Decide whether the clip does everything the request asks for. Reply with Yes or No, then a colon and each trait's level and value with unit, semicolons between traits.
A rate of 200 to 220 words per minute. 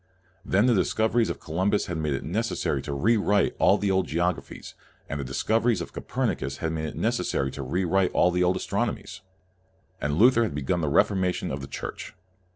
Yes: fast, 205 wpm